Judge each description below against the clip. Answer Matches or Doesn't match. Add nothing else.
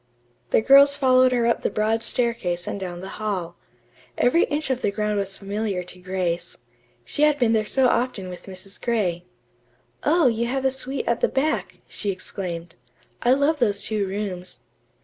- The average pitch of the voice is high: Matches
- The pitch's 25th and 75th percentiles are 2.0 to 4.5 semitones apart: Doesn't match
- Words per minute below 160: Doesn't match